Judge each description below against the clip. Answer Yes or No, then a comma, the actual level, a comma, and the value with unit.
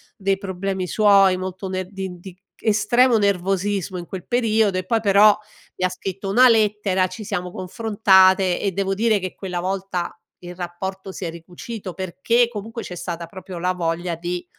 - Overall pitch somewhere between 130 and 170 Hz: No, high, 190 Hz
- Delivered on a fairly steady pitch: Yes, narrow, 2.2 semitones